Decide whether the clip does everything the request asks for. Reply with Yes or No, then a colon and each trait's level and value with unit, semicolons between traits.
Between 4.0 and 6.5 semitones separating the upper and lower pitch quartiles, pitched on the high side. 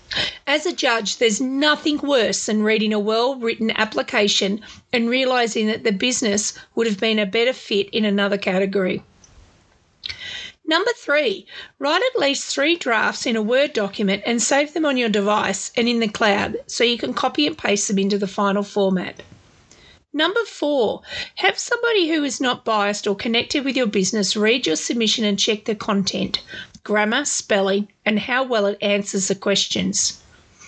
Yes: average, 5.0 semitones; high, 225 Hz